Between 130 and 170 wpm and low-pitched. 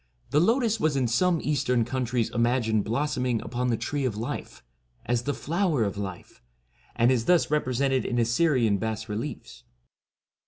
Yes: average, 155 wpm; low, 125 Hz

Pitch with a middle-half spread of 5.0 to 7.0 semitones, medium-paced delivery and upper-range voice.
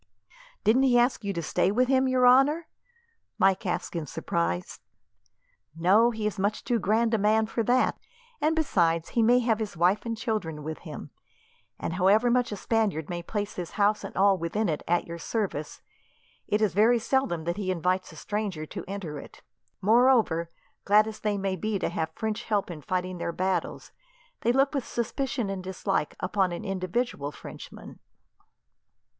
No: average, 4.5 semitones; average, 180 wpm; high, 205 Hz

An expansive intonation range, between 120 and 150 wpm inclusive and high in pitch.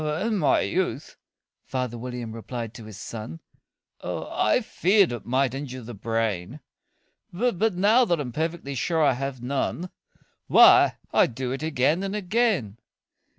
No: wide, 6.7 semitones; average, 145 wpm; low, 135 Hz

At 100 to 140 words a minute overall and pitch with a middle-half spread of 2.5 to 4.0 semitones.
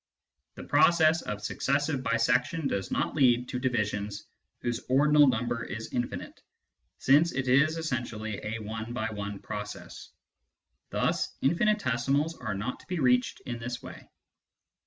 No: slow, 135 wpm; average, 4.4 semitones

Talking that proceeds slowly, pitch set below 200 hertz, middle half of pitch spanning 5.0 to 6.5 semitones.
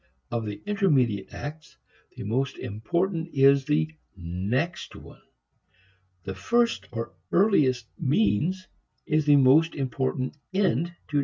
Yes: slow, 125 wpm; medium, 140 Hz; wide, 5.6 semitones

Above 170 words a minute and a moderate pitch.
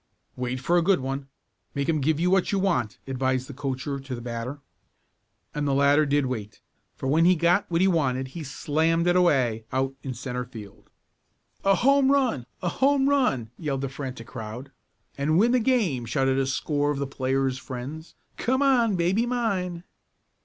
Yes: average, 185 wpm; medium, 145 Hz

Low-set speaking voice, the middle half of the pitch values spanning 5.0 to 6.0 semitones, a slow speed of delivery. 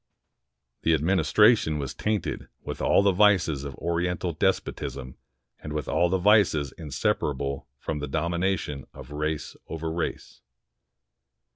No: very low, 80 Hz; average, 4.1 semitones; slow, 125 wpm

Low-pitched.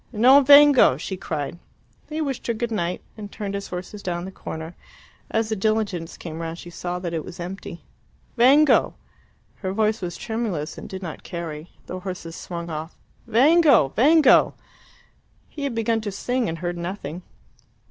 No: high, 195 Hz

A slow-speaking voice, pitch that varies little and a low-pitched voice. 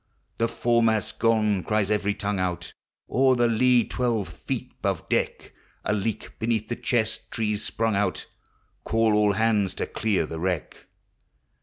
No: average, 160 wpm; narrow, 2.1 semitones; low, 110 Hz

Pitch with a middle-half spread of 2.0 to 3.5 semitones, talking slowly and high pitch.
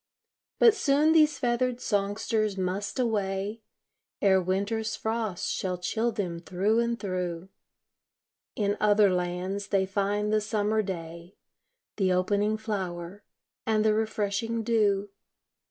Yes: narrow, 2.6 semitones; slow, 120 wpm; high, 205 Hz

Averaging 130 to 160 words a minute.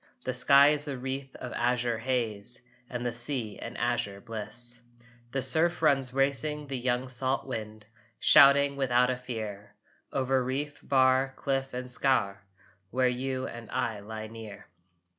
Yes: average, 150 wpm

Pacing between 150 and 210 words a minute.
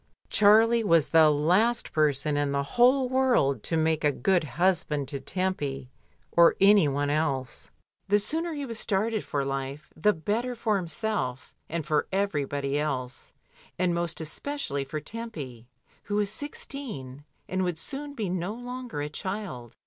Yes: average, 155 wpm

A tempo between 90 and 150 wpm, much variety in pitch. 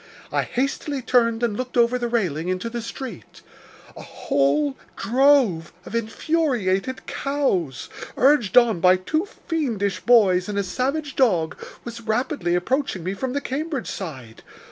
Yes: average, 145 wpm; wide, 6.2 semitones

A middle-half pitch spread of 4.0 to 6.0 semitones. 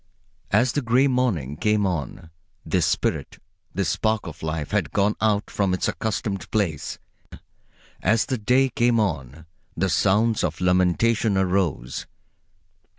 Yes: average, 4.7 semitones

